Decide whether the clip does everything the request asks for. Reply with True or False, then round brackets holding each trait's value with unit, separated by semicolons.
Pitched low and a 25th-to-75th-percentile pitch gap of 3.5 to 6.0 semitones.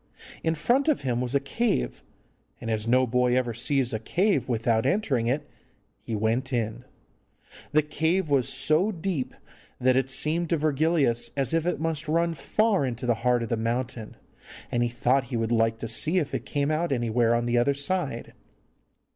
True (130 Hz; 4.8 semitones)